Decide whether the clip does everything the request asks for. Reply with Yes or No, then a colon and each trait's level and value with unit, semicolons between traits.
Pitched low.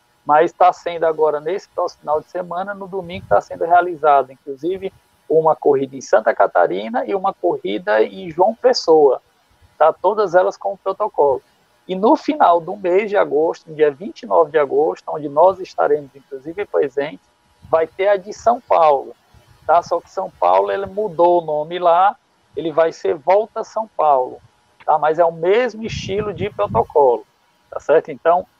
No: medium, 185 Hz